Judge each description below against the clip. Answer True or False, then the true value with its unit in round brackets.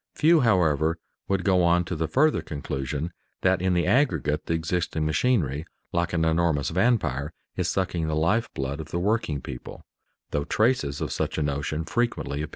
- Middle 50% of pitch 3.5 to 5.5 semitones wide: True (3.9 semitones)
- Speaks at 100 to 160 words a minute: False (175 wpm)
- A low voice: True (85 Hz)